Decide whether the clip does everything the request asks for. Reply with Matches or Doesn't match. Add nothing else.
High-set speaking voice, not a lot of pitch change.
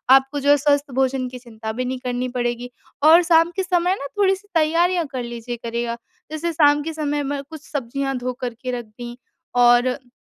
Doesn't match